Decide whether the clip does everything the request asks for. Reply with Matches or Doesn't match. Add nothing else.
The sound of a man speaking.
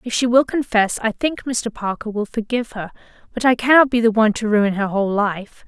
Doesn't match